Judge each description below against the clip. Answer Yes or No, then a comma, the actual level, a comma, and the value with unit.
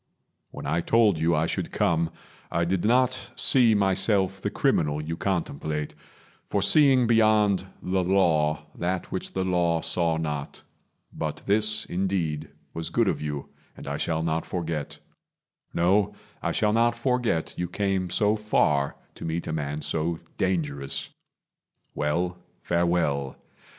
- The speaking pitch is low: Yes, very low, 85 Hz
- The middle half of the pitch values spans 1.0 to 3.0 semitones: No, average, 4.2 semitones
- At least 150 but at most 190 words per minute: No, average, 140 wpm